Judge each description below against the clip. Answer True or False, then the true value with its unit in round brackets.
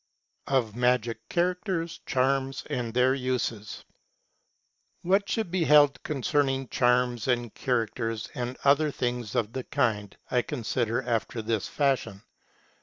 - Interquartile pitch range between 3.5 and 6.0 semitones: False (3.1 semitones)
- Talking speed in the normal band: False (125 wpm)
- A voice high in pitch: False (125 Hz)